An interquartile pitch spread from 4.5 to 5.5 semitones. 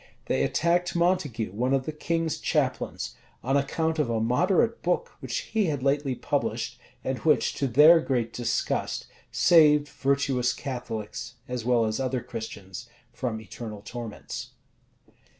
Yes: average, 5.1 semitones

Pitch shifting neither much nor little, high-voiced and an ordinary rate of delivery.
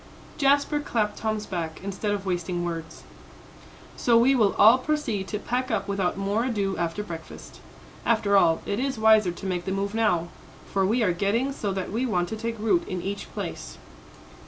Yes: average, 3.6 semitones; high, 205 Hz; average, 185 wpm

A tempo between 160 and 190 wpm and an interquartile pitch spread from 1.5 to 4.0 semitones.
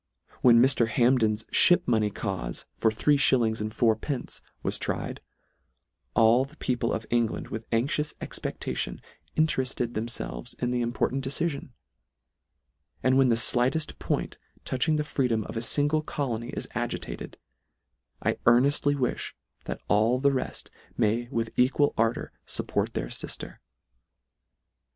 No: average, 150 wpm; average, 3.3 semitones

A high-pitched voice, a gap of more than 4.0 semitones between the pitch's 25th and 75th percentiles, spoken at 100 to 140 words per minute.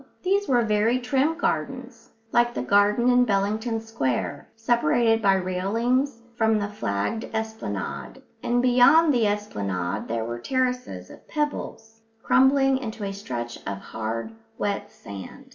Yes: high, 225 Hz; average, 4.5 semitones; slow, 135 wpm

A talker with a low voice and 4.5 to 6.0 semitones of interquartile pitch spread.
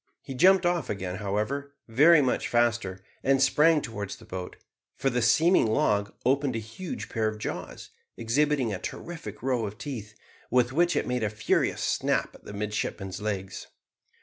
Yes: low, 120 Hz; average, 5.1 semitones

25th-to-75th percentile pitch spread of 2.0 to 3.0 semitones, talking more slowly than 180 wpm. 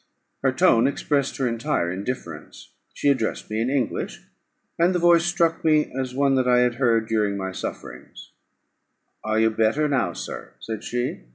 No: average, 4.4 semitones; average, 170 wpm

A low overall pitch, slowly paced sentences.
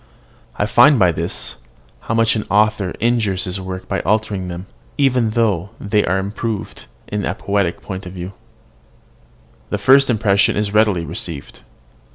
No: low, 100 Hz; average, 155 wpm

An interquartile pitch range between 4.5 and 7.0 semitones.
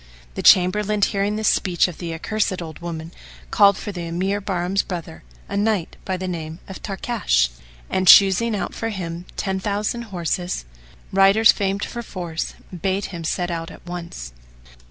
No: average, 2.9 semitones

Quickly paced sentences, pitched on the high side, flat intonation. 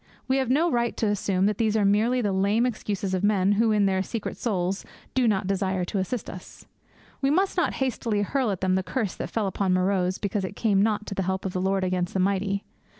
No: fast, 240 wpm; high, 200 Hz; average, 3.0 semitones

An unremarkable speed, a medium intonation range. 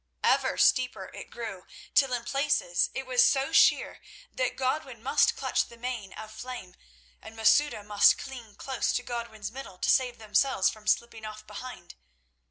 Yes: average, 165 wpm; average, 3.4 semitones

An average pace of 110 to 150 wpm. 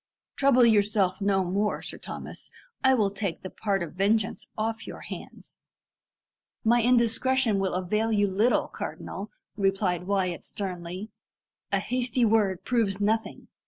Yes: slow, 135 wpm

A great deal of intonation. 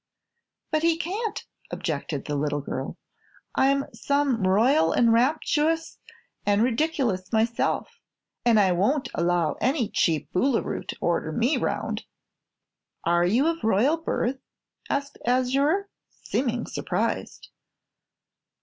Yes: wide, 7.5 semitones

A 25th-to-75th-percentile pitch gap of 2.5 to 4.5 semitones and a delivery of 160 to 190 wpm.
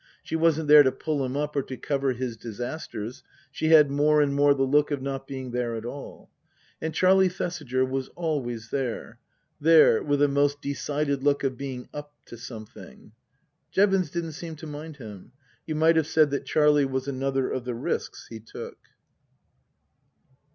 Yes: average, 2.8 semitones; average, 180 wpm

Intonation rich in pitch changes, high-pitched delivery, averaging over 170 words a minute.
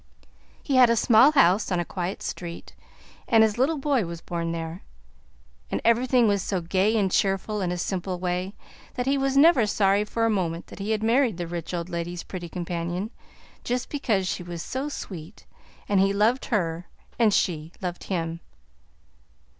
No: average, 4.8 semitones; high, 195 Hz; average, 180 wpm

